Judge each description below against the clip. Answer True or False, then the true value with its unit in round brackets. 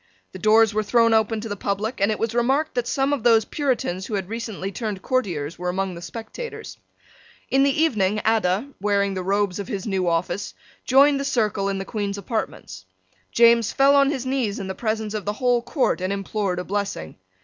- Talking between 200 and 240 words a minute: True (205 wpm)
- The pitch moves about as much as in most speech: True (3.6 semitones)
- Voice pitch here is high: True (215 Hz)